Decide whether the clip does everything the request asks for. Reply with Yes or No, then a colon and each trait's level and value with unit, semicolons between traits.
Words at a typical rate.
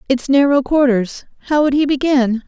Yes: average, 170 wpm